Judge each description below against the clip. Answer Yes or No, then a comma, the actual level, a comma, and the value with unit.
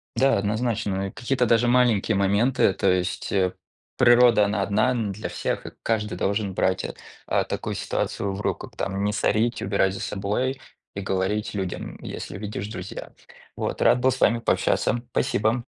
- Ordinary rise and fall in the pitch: Yes, average, 3.4 semitones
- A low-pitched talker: Yes, low, 105 Hz